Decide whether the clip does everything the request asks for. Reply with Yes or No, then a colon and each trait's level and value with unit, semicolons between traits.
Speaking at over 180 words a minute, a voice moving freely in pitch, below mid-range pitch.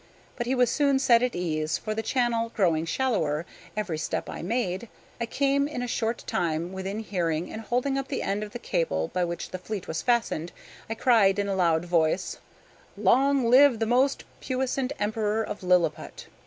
No: average, 190 wpm; wide, 5.8 semitones; high, 215 Hz